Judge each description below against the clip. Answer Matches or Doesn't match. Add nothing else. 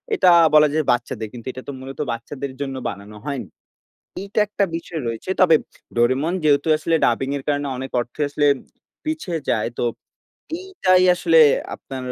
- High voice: Doesn't match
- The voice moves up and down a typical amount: Matches